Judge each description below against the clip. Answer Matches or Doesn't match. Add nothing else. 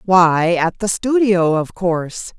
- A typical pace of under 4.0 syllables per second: Matches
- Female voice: Matches